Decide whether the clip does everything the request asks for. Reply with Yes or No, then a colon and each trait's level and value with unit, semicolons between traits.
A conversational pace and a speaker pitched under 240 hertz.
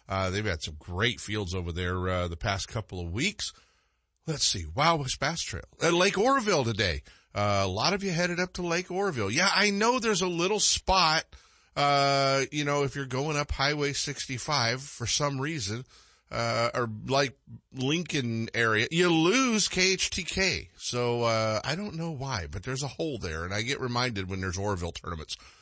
Yes: average, 185 wpm; low, 135 Hz